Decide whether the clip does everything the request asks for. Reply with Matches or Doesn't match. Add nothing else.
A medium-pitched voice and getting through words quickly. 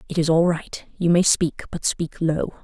Matches